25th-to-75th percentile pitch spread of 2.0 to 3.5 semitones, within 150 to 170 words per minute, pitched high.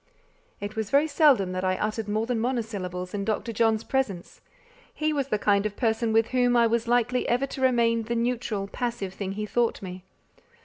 No: average, 3.2 semitones; average, 195 wpm; high, 225 Hz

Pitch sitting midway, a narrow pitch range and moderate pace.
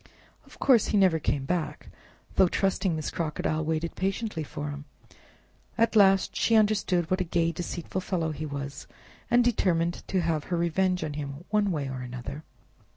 No: medium, 170 Hz; average, 3.9 semitones; average, 170 wpm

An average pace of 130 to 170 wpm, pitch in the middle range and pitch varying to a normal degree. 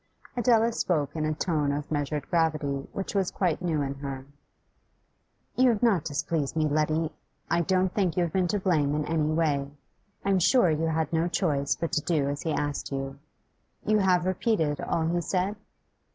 No: average, 190 wpm; medium, 160 Hz; average, 3.9 semitones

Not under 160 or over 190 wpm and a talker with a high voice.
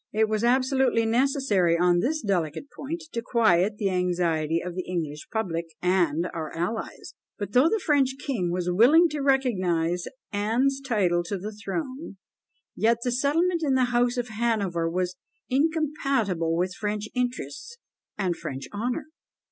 No: average, 150 wpm; high, 215 Hz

